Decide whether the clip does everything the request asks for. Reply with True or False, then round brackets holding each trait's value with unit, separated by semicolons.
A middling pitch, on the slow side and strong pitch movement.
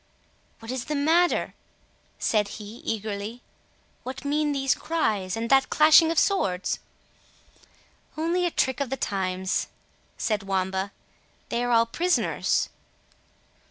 False (240 Hz; 125 wpm; 6.9 semitones)